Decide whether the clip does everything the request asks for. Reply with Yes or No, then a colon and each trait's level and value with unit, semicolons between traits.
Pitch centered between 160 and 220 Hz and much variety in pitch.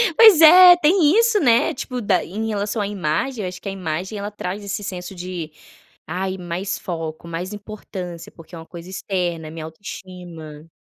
No: medium, 185 Hz; average, 3.9 semitones